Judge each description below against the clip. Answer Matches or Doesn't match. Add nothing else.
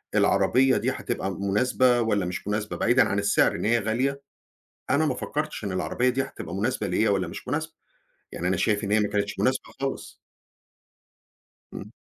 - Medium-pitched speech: Doesn't match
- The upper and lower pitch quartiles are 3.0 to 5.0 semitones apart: Matches